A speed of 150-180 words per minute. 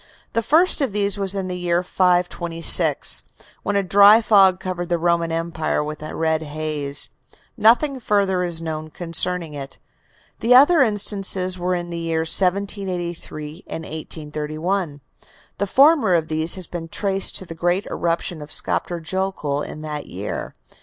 Yes: average, 155 wpm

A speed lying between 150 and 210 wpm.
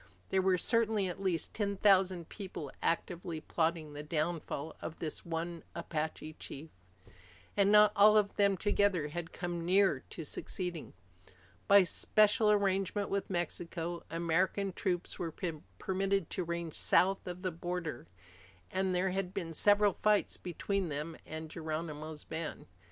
No: average, 140 wpm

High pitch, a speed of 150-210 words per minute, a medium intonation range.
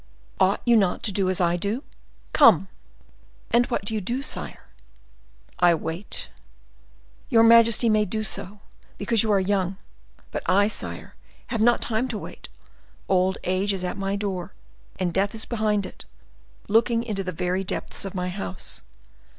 Yes: high, 200 Hz; average, 165 wpm; average, 3.1 semitones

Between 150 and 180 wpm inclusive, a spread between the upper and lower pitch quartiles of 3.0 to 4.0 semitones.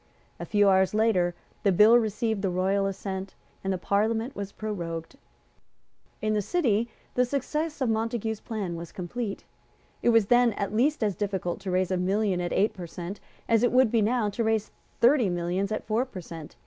No: average, 190 wpm; average, 3.4 semitones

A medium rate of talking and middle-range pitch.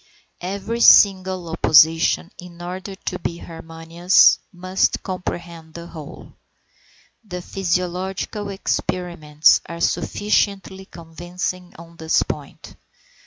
No: slow, 95 wpm; medium, 175 Hz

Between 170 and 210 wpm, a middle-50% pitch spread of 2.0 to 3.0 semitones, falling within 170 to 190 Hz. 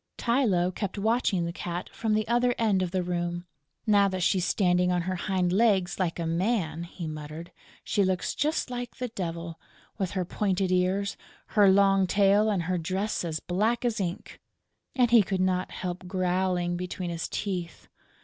Yes: average, 180 wpm; average, 2.7 semitones; medium, 185 Hz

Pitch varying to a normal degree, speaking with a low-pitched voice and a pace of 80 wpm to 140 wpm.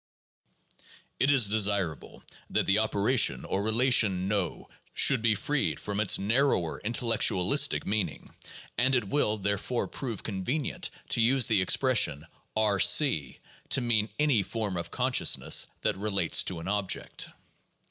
Yes: average, 3.9 semitones; low, 105 Hz; slow, 135 wpm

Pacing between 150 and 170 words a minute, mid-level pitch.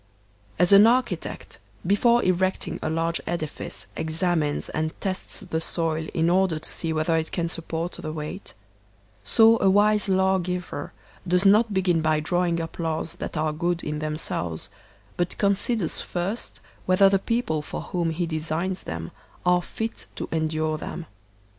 Yes: average, 155 wpm; medium, 170 Hz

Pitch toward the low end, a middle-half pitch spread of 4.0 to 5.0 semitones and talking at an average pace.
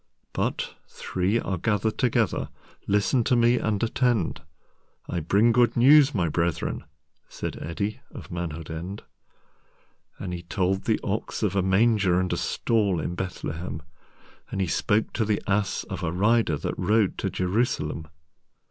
No: low, 100 Hz; average, 4.3 semitones; slow, 125 wpm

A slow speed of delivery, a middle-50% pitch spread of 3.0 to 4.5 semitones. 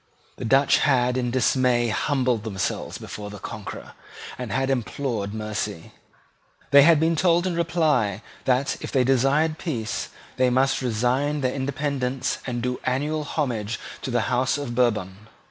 No: average, 150 wpm; average, 3.5 semitones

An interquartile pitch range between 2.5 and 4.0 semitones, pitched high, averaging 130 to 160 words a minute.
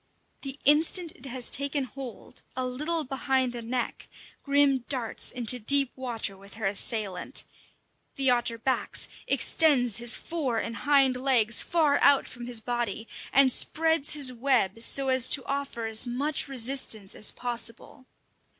Yes: average, 3.1 semitones; very high, 255 Hz; average, 150 wpm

